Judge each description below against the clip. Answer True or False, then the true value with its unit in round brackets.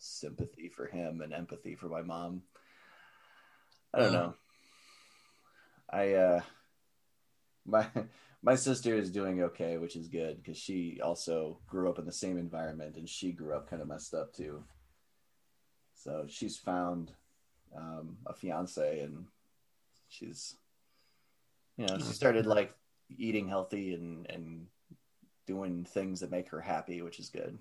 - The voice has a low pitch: True (90 Hz)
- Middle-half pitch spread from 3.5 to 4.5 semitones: False (2.8 semitones)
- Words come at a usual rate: True (145 wpm)